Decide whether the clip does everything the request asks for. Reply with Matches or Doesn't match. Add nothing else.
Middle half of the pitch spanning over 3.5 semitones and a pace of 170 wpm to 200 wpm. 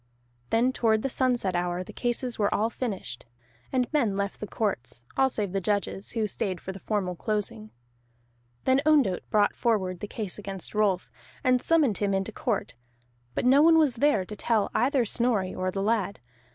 Matches